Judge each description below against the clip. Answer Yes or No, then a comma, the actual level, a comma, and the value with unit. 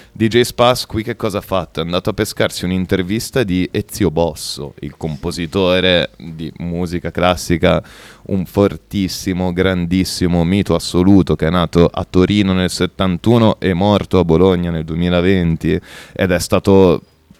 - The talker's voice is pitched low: Yes, very low, 90 Hz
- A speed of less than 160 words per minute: Yes, average, 140 wpm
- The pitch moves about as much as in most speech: No, narrow, 2.3 semitones